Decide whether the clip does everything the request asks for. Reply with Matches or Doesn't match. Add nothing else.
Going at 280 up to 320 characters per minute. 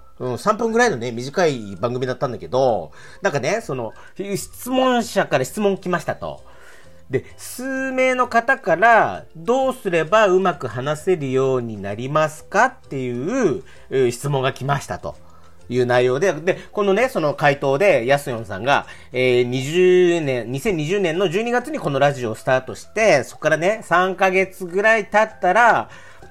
Matches